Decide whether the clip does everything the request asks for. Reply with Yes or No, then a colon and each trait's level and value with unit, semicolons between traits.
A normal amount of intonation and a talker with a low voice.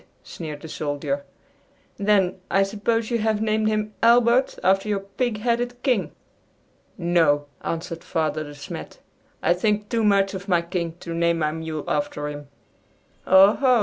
No: average, 5.0 semitones; high, 195 Hz